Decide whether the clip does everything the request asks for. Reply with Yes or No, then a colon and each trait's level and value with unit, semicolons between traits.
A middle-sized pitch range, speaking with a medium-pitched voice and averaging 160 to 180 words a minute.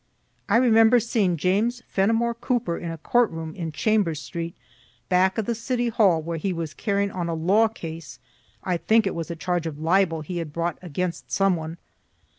No: average, 5.0 semitones; medium, 180 Hz; average, 195 wpm